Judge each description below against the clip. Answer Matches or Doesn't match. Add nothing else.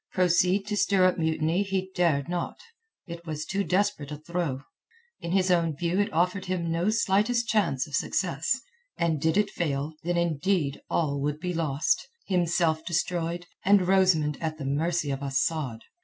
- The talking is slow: Doesn't match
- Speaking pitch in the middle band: Matches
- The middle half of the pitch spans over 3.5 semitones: Doesn't match